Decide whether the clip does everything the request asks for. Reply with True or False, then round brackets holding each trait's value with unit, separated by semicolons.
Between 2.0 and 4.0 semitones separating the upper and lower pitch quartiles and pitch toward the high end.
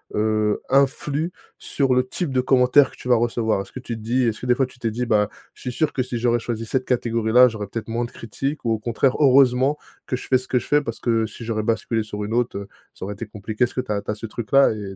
False (2.8 semitones; 120 Hz)